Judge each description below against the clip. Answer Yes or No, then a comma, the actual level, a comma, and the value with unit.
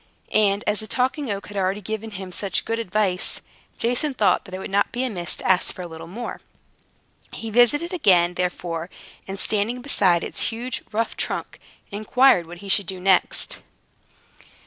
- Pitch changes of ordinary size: Yes, average, 3.9 semitones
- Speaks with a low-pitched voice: No, high, 205 Hz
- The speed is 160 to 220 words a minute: Yes, average, 180 wpm